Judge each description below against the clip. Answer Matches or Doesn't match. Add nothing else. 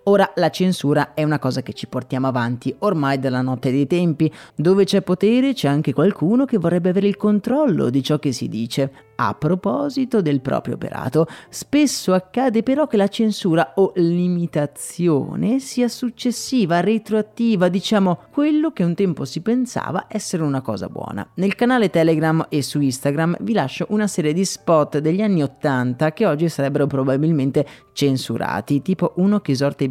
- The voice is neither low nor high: Matches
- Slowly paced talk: Doesn't match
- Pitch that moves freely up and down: Matches